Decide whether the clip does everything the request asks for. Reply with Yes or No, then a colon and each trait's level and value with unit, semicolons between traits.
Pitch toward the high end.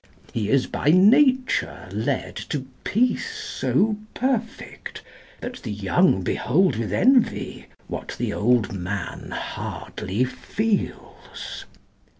No: medium, 180 Hz